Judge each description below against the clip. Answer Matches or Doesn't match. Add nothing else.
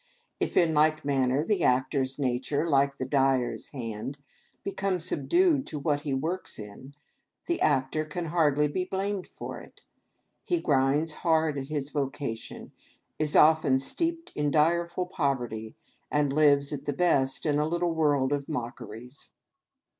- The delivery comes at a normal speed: Matches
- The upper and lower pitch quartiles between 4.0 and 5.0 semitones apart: Doesn't match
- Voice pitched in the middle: Matches